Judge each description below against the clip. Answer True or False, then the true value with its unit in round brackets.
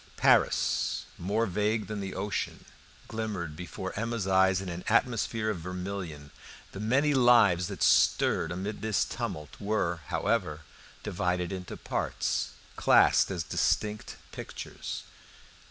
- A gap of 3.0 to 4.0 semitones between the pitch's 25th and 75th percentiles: True (3.3 semitones)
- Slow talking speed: True (120 wpm)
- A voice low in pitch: True (95 Hz)